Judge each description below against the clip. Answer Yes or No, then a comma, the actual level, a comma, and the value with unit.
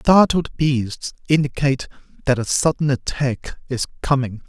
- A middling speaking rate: No, slow, 120 wpm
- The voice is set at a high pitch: No, low, 135 Hz